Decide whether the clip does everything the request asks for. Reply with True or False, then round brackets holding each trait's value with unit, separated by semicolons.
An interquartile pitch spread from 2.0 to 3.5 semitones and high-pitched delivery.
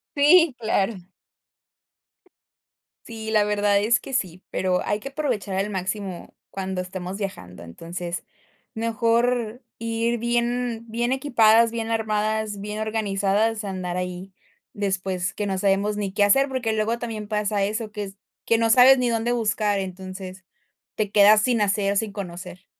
True (2.9 semitones; 210 Hz)